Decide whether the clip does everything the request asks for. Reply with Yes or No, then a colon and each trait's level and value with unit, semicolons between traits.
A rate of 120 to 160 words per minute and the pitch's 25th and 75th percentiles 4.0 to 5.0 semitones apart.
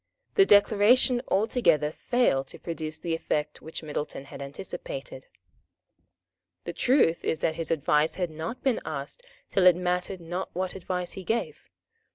No: average, 150 wpm; wide, 5.5 semitones